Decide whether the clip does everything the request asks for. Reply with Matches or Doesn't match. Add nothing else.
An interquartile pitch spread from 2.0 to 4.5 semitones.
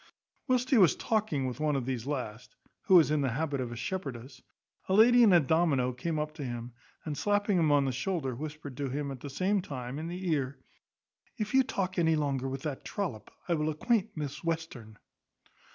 Doesn't match